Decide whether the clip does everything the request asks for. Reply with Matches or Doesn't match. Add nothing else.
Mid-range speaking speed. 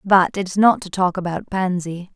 Matches